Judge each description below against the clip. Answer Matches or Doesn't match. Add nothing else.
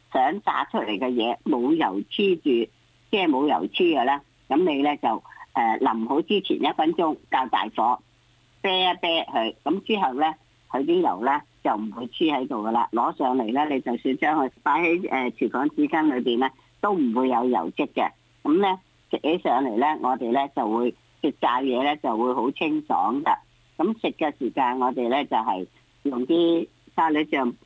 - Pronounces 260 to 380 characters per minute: Doesn't match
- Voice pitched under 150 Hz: Doesn't match